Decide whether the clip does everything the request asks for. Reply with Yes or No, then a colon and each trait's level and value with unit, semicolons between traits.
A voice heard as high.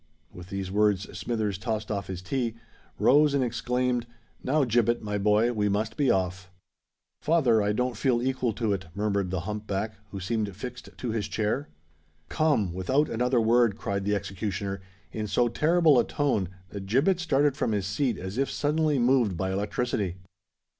No: low, 110 Hz